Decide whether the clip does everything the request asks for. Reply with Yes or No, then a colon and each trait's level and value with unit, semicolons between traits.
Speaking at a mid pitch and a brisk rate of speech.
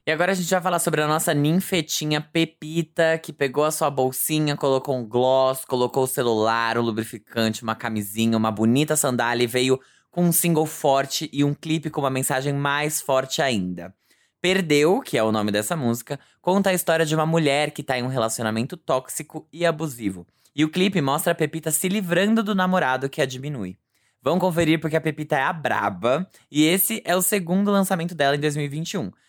Yes: medium, 150 Hz; fast, 195 wpm